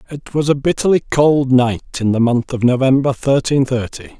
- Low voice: Yes, low, 130 Hz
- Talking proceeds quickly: No, average, 185 wpm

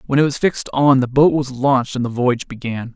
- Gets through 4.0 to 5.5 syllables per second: No, 6.1 syllables/s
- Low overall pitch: Yes, low, 130 Hz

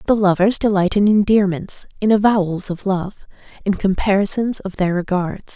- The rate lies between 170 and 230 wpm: No, average, 150 wpm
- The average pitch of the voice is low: No, high, 195 Hz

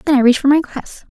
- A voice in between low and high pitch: No, very high, 275 Hz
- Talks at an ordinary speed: No, fast, 310 wpm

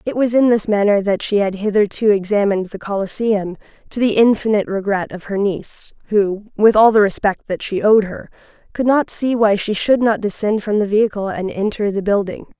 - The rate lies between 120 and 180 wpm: No, average, 195 wpm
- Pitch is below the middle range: No, high, 205 Hz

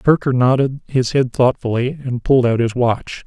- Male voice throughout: Yes, male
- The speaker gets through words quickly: No, average, 185 wpm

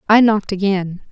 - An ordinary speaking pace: Yes, average, 160 wpm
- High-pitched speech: Yes, high, 200 Hz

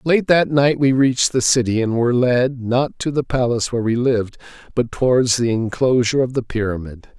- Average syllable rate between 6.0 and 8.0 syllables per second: No, 5.5 syllables/s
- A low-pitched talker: Yes, low, 125 Hz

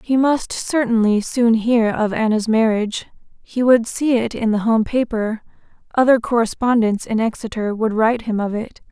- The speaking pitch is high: Yes, high, 225 Hz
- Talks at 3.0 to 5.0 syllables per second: Yes, 4.8 syllables/s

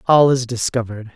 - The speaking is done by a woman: No, male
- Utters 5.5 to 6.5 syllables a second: Yes, 6.0 syllables/s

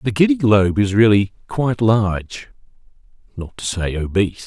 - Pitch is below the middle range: Yes, low, 110 Hz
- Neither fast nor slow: Yes, average, 150 wpm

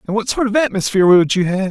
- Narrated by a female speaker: No, male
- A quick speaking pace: Yes, fast, 280 wpm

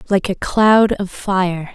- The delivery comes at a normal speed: Yes, average, 170 wpm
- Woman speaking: Yes, female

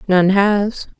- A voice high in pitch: Yes, high, 200 Hz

